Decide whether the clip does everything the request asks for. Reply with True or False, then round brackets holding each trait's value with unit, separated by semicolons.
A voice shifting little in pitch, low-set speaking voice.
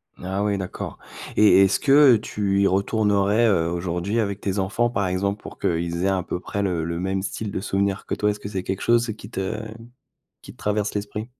True (1.9 semitones; 100 Hz)